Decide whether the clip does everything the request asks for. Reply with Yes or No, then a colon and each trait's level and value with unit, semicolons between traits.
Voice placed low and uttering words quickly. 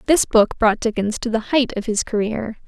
No: high, 225 Hz; fast, 225 wpm